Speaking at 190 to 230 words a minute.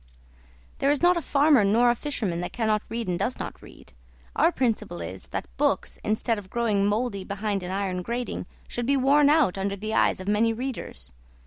Yes: average, 200 wpm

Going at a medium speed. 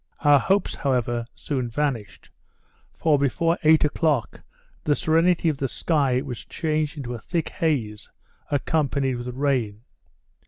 No: slow, 130 wpm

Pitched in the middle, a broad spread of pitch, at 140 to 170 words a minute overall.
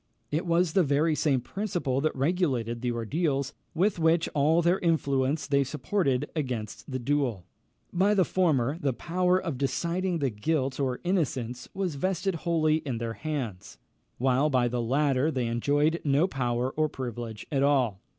No: medium, 145 Hz; average, 4.7 semitones; average, 160 wpm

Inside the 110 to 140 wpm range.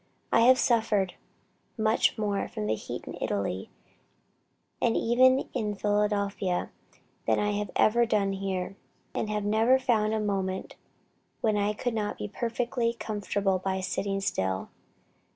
Yes: slow, 135 wpm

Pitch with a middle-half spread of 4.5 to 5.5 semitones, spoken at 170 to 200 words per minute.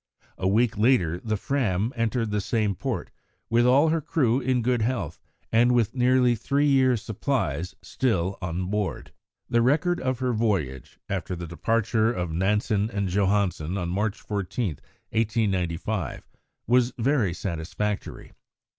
No: average, 4.8 semitones; average, 140 wpm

